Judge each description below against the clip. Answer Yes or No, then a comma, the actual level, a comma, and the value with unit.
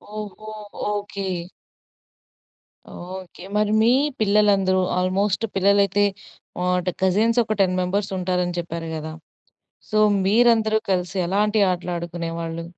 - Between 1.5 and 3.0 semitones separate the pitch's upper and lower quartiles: Yes, average, 2.7 semitones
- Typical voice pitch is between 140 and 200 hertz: Yes, high, 190 Hz